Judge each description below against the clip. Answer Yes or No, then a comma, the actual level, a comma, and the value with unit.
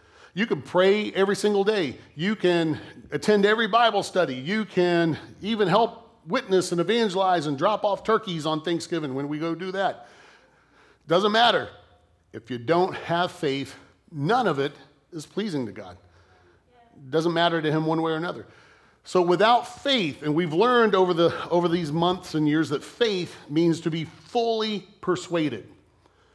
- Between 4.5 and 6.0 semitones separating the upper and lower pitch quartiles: Yes, average, 5.2 semitones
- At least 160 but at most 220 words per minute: Yes, average, 165 wpm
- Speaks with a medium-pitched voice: Yes, medium, 170 Hz